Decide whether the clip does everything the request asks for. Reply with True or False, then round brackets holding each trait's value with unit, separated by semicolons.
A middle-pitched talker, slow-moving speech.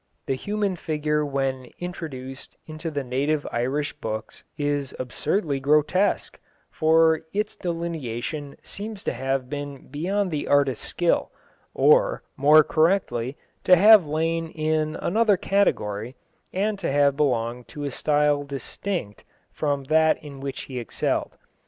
True (150 Hz; 130 wpm)